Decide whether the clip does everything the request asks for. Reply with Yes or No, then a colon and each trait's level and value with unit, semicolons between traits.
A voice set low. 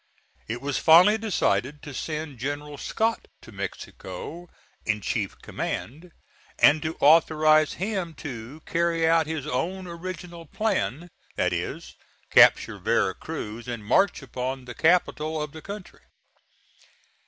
No: medium, 155 Hz